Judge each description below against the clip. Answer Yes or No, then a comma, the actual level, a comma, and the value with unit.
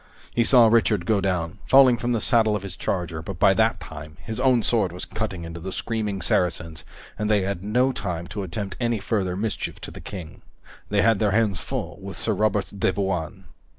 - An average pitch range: Yes, average, 3.8 semitones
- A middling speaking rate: No, fast, 210 wpm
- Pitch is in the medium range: No, low, 100 Hz